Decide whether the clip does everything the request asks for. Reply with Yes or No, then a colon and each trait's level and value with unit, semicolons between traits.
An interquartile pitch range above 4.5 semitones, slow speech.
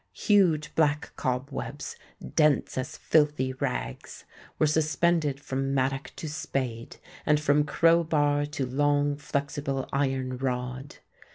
No: narrow, 2.4 semitones; slow, 120 wpm